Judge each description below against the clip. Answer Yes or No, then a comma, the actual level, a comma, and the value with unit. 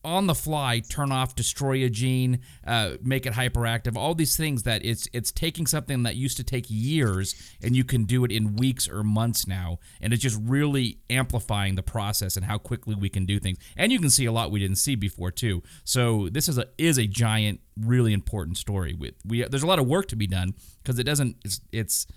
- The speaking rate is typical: No, fast, 235 wpm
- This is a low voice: Yes, low, 115 Hz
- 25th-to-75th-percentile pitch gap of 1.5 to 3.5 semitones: No, average, 4.3 semitones